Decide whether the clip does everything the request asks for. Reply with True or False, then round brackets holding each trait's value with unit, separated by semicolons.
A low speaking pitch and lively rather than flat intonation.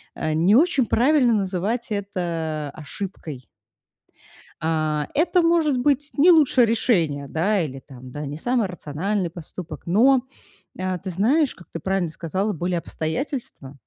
False (185 Hz; 7.6 semitones)